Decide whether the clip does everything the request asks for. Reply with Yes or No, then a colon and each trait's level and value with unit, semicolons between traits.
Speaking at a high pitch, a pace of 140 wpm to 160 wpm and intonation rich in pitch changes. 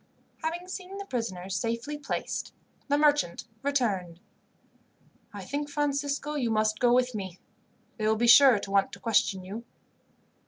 Yes: high, 240 Hz; average, 150 wpm; wide, 5.9 semitones